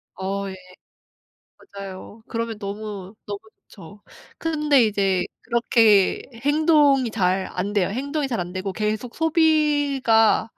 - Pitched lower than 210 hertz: No, high, 220 Hz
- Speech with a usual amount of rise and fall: No, wide, 5.9 semitones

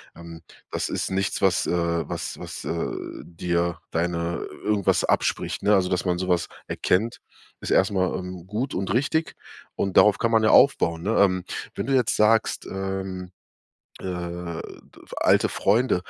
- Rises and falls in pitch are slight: No, average, 3.1 semitones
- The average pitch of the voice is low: Yes, very low, 95 Hz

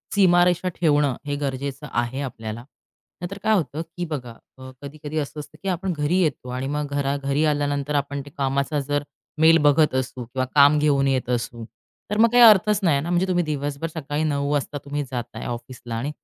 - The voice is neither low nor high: Yes, medium, 145 Hz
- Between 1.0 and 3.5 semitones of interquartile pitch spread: Yes, average, 2.9 semitones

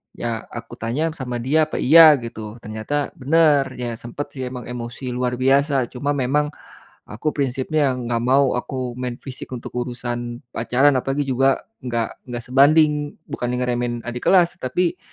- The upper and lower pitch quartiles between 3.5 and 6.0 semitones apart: No, average, 3.1 semitones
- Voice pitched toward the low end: Yes, low, 130 Hz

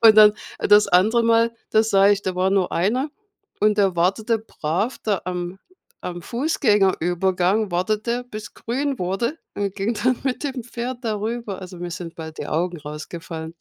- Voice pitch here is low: No, high, 205 Hz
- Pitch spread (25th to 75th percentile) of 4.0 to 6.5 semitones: Yes, average, 4.3 semitones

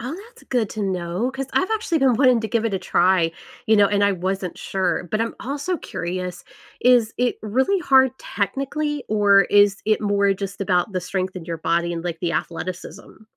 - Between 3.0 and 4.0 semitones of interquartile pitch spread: No, average, 5.3 semitones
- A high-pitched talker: Yes, high, 205 Hz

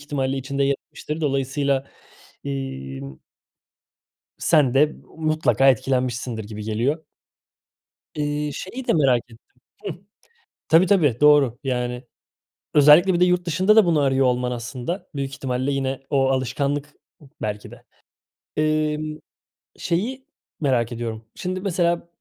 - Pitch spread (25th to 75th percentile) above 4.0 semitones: No, average, 3.7 semitones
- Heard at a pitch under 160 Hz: Yes, medium, 140 Hz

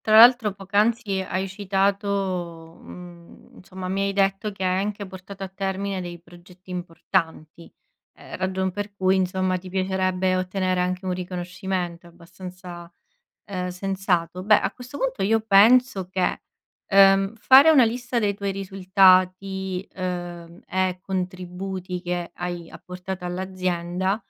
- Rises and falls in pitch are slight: Yes, narrow, 1.5 semitones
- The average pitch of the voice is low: No, high, 190 Hz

